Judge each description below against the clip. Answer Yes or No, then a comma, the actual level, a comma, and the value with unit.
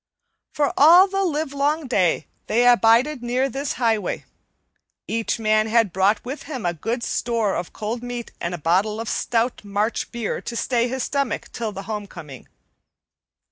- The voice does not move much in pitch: No, average, 3.9 semitones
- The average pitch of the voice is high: Yes, high, 230 Hz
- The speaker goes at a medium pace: Yes, average, 160 wpm